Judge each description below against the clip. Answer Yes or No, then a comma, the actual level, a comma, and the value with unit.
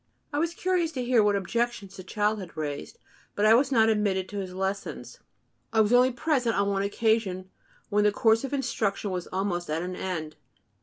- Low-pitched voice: No, high, 210 Hz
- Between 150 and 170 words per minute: No, average, 200 wpm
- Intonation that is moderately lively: Yes, average, 4.1 semitones